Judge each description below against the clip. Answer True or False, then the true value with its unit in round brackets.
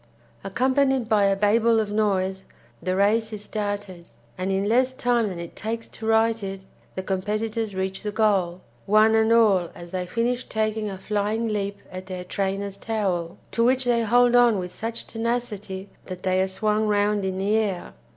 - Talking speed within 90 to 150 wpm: False (180 wpm)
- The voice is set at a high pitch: True (210 Hz)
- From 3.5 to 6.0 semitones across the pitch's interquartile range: False (2.9 semitones)